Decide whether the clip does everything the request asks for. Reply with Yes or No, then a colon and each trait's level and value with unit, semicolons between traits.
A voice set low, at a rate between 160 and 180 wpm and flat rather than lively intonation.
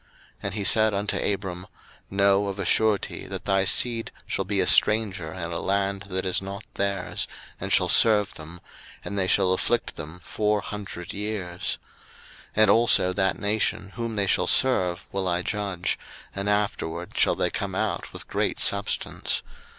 Yes: low, 100 Hz; average, 175 wpm; narrow, 2.0 semitones